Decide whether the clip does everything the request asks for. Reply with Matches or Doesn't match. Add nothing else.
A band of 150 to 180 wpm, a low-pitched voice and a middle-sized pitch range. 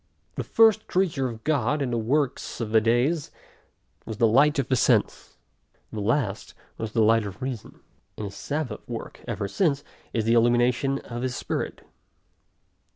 Matches